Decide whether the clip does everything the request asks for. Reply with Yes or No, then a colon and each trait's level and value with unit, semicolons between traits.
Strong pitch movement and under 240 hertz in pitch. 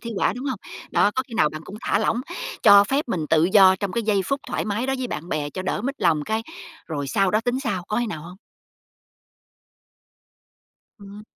No: average, 5.0 semitones; high, 205 Hz